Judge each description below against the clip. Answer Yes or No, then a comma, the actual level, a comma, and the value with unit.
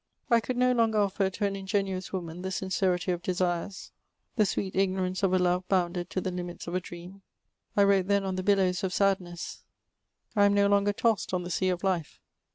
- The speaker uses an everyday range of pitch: No, narrow, 1.8 semitones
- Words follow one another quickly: Yes, fast, 210 wpm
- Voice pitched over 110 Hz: Yes, high, 190 Hz